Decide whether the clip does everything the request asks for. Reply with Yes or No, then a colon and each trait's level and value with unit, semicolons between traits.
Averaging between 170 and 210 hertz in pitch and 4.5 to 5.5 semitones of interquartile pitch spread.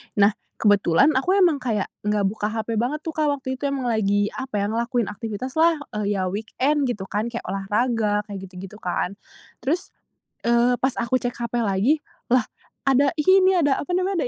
No: high, 235 Hz; average, 5.2 semitones